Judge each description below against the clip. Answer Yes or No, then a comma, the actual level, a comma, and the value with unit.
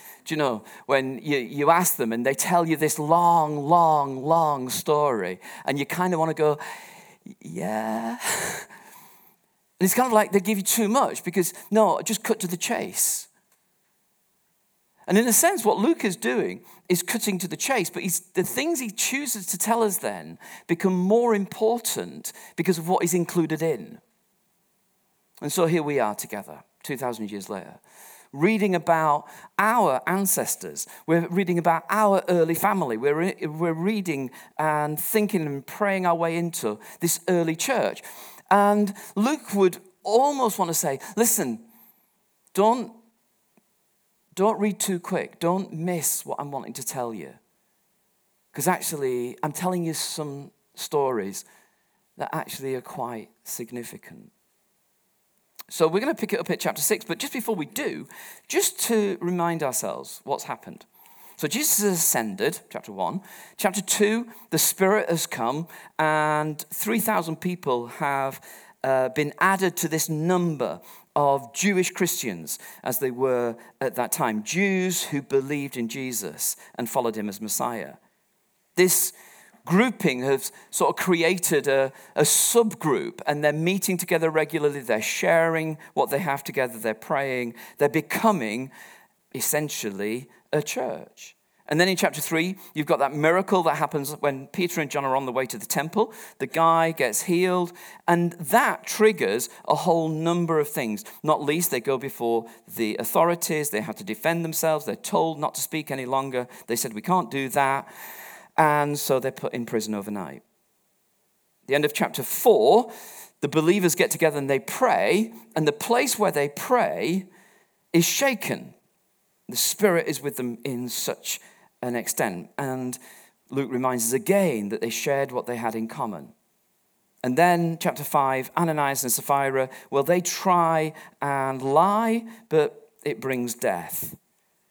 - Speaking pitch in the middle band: Yes, medium, 165 Hz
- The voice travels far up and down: Yes, wide, 5.8 semitones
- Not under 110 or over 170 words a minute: Yes, average, 155 wpm